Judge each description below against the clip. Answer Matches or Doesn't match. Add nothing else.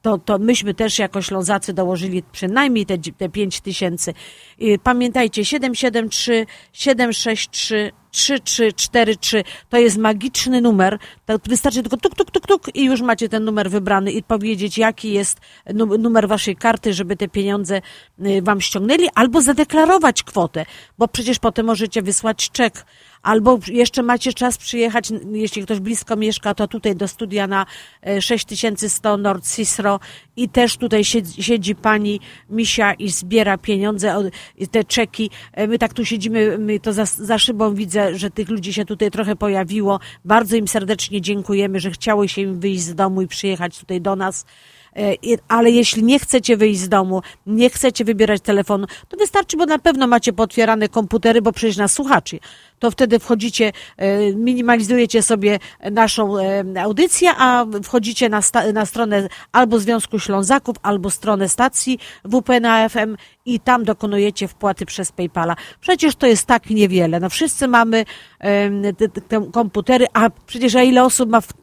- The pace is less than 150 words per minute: Doesn't match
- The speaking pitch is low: Doesn't match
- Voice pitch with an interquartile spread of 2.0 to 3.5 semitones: Matches